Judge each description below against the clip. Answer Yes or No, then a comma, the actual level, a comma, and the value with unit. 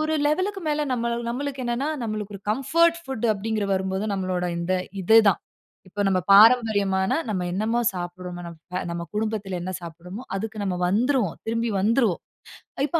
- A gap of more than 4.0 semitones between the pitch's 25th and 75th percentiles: Yes, average, 4.5 semitones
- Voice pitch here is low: No, high, 215 Hz